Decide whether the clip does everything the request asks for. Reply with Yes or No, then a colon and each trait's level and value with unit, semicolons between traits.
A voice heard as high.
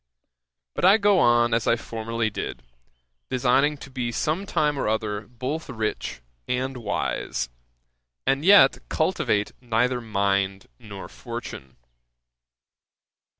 No: low, 120 Hz